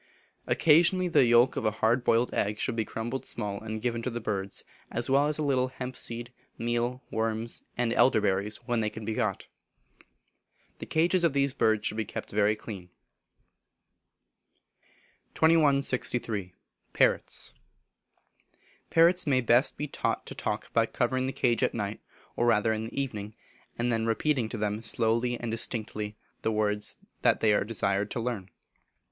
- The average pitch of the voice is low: Yes, low, 115 Hz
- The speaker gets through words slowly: No, average, 165 wpm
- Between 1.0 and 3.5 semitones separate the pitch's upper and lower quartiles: Yes, average, 3.1 semitones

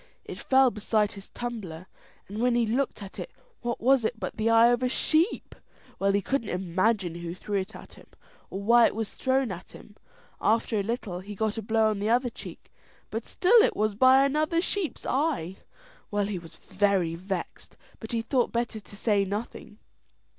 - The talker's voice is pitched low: No, high, 220 Hz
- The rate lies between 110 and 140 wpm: No, average, 195 wpm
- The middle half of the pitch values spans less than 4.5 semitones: Yes, average, 3.5 semitones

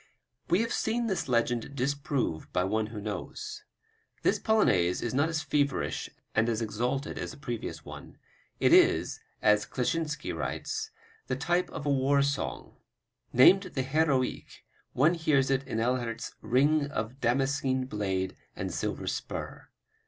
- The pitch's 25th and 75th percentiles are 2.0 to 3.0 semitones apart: No, average, 4.4 semitones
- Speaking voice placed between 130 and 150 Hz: Yes, low, 135 Hz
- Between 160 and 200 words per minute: No, average, 145 wpm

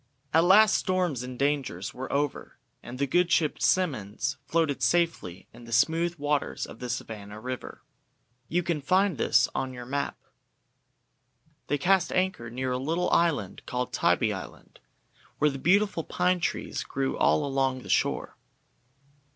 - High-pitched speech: No, medium, 140 Hz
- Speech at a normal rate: Yes, average, 150 wpm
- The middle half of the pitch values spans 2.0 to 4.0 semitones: No, wide, 5.4 semitones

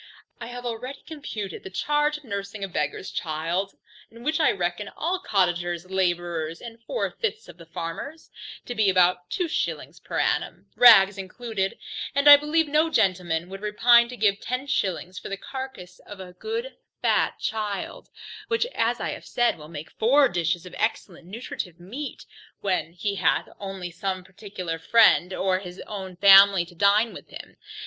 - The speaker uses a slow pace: No, average, 175 wpm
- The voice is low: No, high, 200 Hz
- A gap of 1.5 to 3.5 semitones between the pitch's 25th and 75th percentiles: No, average, 5.3 semitones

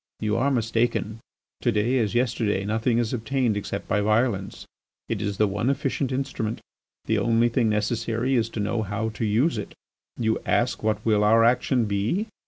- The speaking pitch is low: Yes, low, 115 Hz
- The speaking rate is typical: Yes, average, 180 wpm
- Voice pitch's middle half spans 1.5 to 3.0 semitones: Yes, narrow, 2.5 semitones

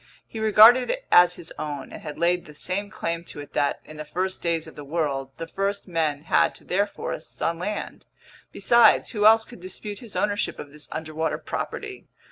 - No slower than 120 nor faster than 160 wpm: No, fast, 205 wpm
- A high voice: No, medium, 175 Hz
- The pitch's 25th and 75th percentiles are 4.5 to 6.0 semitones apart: Yes, average, 5.0 semitones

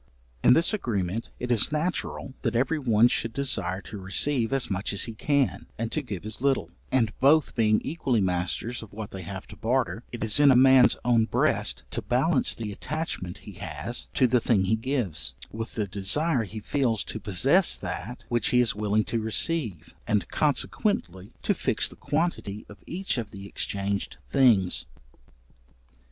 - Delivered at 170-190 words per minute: Yes, average, 180 wpm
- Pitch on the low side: Yes, low, 115 Hz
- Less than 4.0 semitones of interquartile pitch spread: No, average, 4.8 semitones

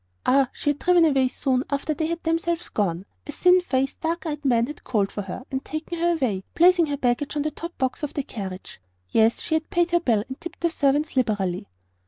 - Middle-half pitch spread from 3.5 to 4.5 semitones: No, average, 5.1 semitones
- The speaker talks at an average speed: No, fast, 225 wpm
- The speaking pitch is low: No, very high, 290 Hz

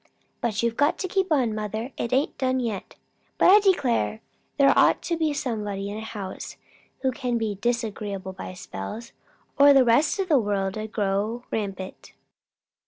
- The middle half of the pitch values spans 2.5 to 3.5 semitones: No, average, 4.8 semitones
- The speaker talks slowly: No, average, 170 wpm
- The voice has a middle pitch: No, high, 230 Hz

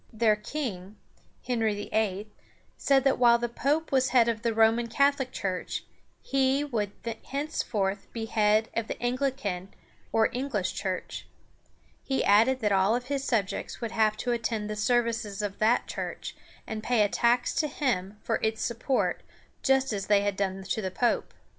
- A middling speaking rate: Yes, average, 165 wpm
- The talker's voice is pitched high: Yes, high, 225 Hz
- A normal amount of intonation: Yes, average, 3.5 semitones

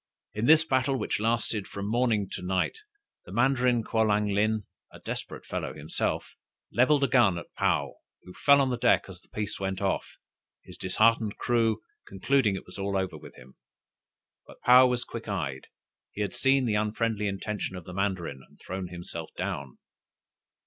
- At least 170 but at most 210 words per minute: Yes, average, 175 wpm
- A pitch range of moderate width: Yes, average, 4.1 semitones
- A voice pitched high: No, low, 105 Hz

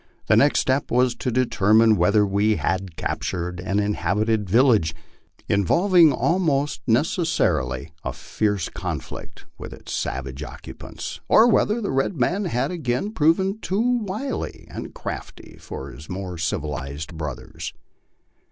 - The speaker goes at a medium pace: No, slow, 130 wpm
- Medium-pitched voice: No, low, 110 Hz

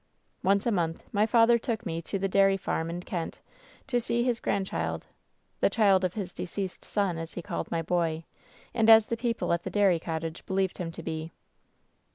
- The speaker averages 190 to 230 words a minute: Yes, fast, 205 wpm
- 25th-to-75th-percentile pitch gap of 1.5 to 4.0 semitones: No, average, 4.5 semitones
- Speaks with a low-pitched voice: No, high, 190 Hz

